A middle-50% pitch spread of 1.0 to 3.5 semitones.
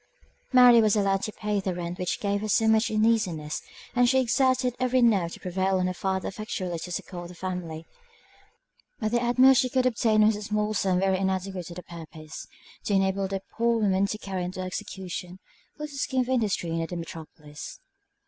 No: average, 4.0 semitones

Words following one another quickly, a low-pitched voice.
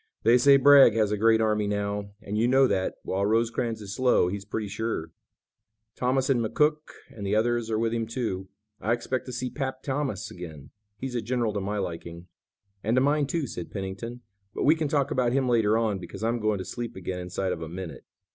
Yes: fast, 215 wpm; low, 110 Hz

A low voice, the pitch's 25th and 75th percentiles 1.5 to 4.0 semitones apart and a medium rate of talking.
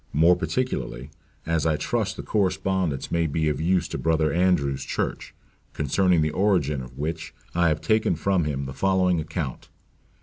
Yes: very low, 80 Hz; average, 3.6 semitones; average, 165 wpm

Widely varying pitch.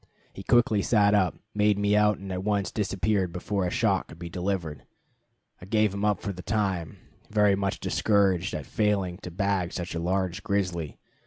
No: narrow, 2.5 semitones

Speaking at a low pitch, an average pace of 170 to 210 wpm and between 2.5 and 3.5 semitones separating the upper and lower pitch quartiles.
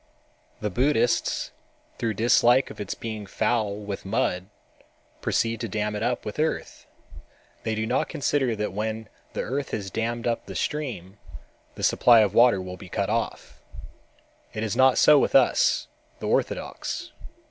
No: low, 110 Hz; average, 160 wpm; average, 2.9 semitones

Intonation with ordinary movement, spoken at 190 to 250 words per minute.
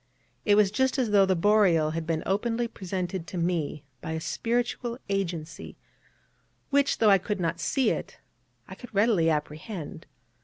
No: average, 4.8 semitones; average, 160 wpm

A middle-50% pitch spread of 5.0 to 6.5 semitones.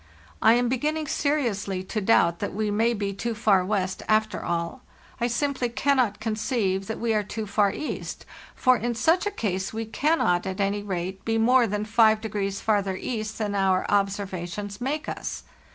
No: average, 3.3 semitones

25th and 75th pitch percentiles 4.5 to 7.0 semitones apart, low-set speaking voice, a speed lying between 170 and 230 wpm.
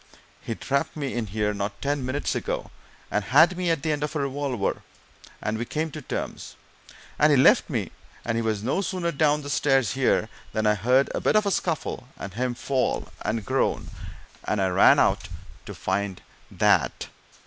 Yes: wide, 5.6 semitones; low, 130 Hz; average, 190 wpm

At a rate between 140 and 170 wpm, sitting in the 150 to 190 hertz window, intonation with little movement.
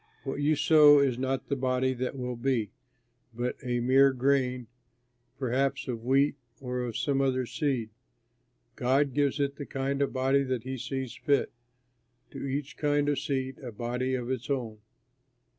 No: average, 165 wpm; low, 130 Hz; narrow, 1.8 semitones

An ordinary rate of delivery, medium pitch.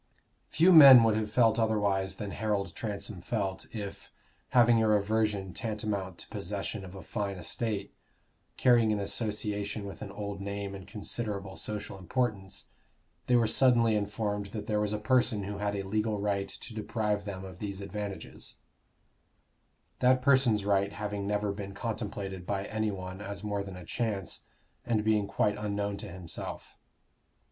No: average, 160 wpm; low, 105 Hz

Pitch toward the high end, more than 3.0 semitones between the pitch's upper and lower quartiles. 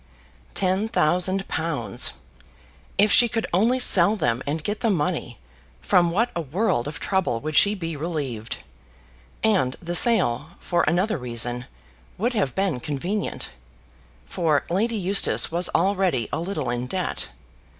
No: medium, 175 Hz; wide, 5.5 semitones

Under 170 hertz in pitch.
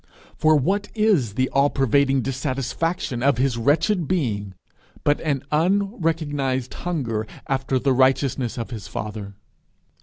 Yes: low, 135 Hz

